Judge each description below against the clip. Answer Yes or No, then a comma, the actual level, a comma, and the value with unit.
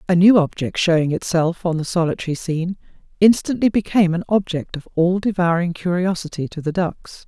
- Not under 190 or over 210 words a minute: No, average, 165 wpm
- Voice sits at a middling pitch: Yes, medium, 175 Hz